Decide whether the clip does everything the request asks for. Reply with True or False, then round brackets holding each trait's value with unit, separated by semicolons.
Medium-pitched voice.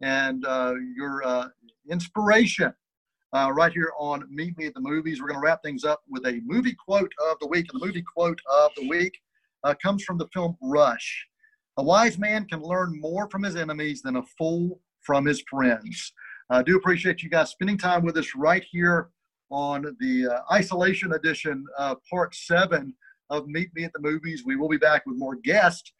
True (160 Hz)